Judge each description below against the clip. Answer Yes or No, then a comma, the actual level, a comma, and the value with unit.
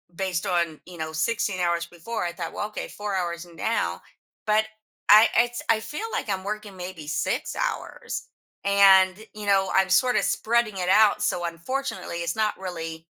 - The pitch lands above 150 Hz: Yes, high, 190 Hz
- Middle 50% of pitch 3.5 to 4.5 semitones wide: Yes, average, 3.8 semitones